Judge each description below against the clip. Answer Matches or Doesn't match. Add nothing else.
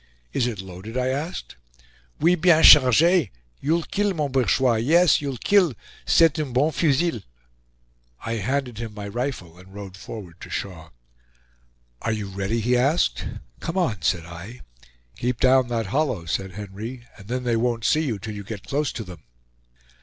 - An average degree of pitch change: Doesn't match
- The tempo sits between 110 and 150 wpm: Doesn't match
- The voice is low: Matches